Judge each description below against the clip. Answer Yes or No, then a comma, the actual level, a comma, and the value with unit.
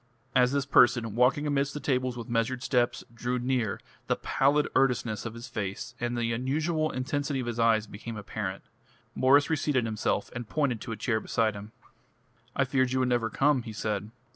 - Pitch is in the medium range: No, low, 125 Hz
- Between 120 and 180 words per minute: No, average, 190 wpm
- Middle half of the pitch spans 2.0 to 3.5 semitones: Yes, average, 2.9 semitones